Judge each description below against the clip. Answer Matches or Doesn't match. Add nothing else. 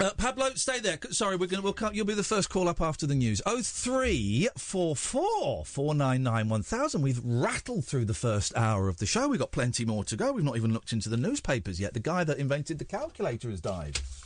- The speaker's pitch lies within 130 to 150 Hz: Matches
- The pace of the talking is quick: Matches